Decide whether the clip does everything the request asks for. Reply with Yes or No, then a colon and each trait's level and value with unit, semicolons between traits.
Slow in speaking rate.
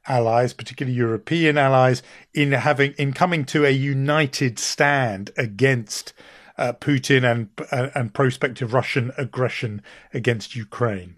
Yes: slow, 120 wpm